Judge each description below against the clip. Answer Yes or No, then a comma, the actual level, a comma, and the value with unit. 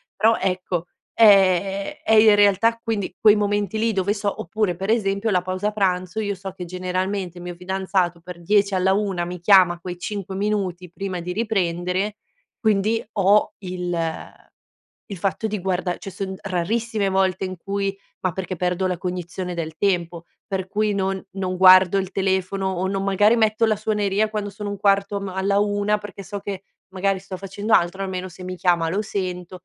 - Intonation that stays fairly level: Yes, narrow, 2.0 semitones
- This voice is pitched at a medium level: No, high, 195 Hz